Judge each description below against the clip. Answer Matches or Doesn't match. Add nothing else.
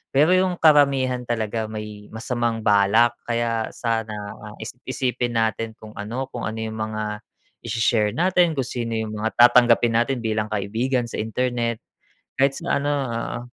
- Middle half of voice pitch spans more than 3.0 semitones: Doesn't match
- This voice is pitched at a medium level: Doesn't match